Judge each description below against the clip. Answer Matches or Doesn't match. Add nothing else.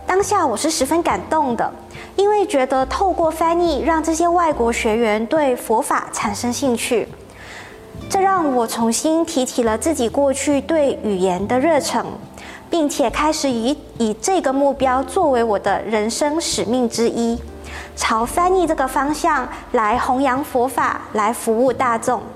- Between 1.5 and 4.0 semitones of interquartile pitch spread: Doesn't match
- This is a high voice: Matches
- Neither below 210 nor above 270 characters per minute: Matches